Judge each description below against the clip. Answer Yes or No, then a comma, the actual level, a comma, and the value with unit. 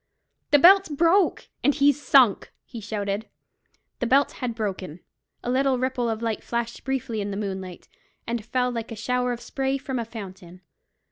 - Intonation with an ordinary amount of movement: Yes, average, 4.0 semitones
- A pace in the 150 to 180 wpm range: Yes, average, 175 wpm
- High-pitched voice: Yes, high, 235 Hz